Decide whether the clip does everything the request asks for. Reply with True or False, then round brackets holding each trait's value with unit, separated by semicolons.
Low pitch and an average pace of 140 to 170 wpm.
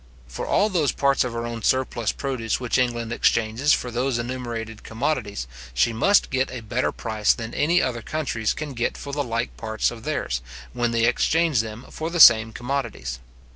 False (120 Hz; 185 wpm)